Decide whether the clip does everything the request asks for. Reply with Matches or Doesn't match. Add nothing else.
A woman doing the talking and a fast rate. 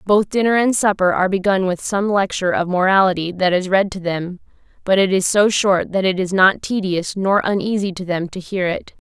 Matches